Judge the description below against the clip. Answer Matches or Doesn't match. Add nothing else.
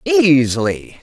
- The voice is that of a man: Doesn't match